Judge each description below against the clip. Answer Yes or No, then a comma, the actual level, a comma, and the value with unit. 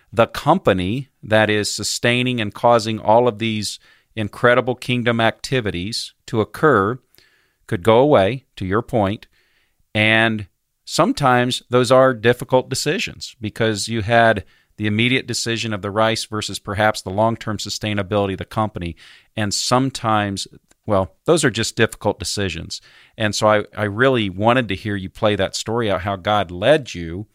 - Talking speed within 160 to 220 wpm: No, average, 150 wpm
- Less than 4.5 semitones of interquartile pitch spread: Yes, average, 2.8 semitones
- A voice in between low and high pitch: No, low, 110 Hz